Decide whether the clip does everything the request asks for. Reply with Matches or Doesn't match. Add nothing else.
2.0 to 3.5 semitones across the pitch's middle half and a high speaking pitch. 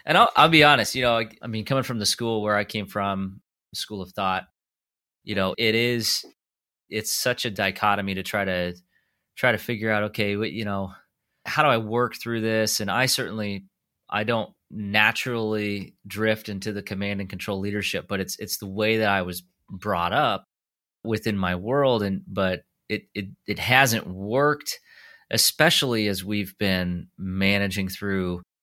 Doesn't match